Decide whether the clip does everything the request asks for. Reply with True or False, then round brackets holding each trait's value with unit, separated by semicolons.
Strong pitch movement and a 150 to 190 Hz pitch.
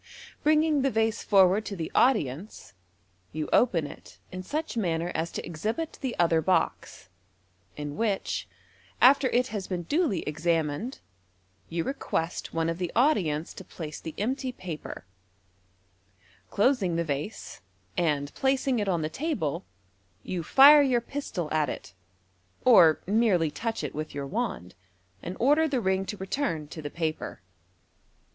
True (7.6 semitones; 185 Hz)